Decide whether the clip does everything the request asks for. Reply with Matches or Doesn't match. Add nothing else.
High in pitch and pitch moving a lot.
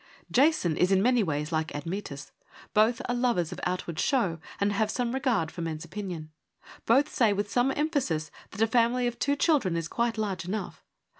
Matches